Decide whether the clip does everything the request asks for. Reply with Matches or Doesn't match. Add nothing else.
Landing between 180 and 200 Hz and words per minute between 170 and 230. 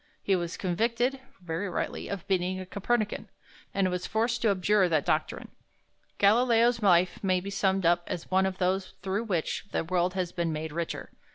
Matches